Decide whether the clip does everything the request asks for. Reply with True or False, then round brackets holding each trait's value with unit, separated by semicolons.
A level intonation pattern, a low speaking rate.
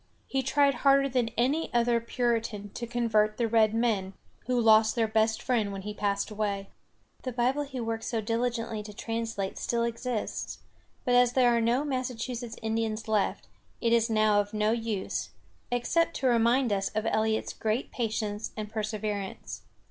False (2.2 semitones; 165 wpm)